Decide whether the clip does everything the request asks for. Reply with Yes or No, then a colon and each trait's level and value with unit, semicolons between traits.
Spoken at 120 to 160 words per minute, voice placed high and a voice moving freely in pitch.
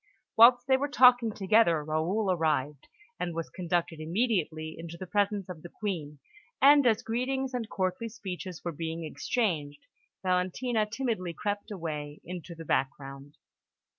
No: average, 140 wpm; medium, 180 Hz; wide, 5.8 semitones